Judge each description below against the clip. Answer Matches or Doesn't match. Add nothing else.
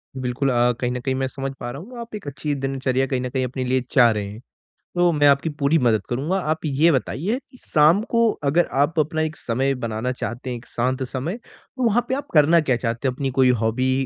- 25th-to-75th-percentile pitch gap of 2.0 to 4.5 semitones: Matches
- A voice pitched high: Doesn't match